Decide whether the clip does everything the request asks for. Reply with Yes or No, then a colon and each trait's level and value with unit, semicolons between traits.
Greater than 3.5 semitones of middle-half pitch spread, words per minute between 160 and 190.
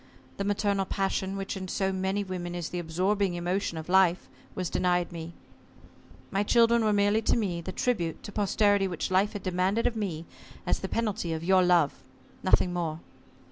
No: narrow, 2.5 semitones; average, 180 wpm